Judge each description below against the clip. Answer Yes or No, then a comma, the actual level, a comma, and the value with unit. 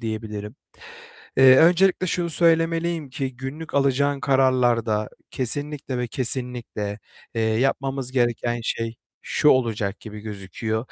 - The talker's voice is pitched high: No, low, 130 Hz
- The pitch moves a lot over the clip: No, average, 4.0 semitones